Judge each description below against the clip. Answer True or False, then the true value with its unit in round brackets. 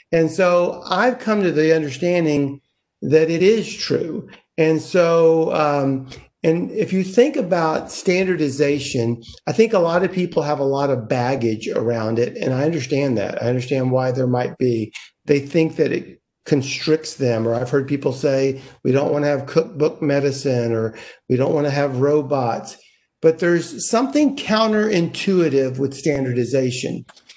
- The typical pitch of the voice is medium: True (150 Hz)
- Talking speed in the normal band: True (160 wpm)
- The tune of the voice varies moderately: True (4.4 semitones)